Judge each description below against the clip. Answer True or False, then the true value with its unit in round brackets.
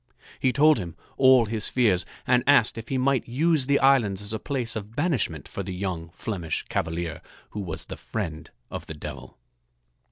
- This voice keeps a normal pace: True (185 wpm)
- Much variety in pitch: True (7.0 semitones)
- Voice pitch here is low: True (110 Hz)